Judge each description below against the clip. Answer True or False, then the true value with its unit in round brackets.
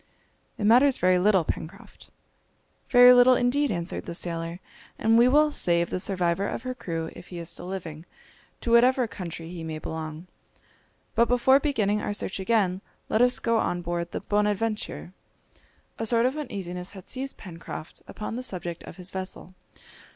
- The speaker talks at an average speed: True (170 wpm)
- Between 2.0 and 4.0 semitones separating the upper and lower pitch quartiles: False (5.5 semitones)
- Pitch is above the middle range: True (195 Hz)